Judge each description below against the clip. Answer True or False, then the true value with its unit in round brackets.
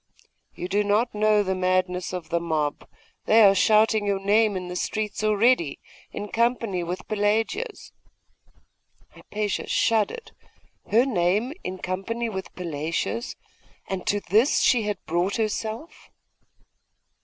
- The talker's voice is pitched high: True (205 Hz)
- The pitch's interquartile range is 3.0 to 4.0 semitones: True (3.3 semitones)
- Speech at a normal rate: False (130 wpm)